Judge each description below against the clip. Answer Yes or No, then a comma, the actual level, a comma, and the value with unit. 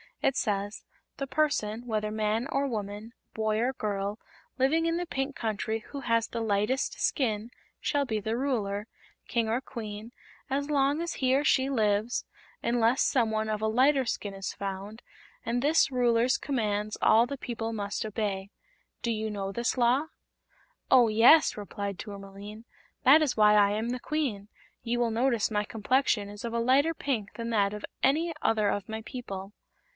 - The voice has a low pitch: No, high, 225 Hz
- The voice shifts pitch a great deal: No, average, 3.8 semitones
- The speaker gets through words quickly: No, average, 175 wpm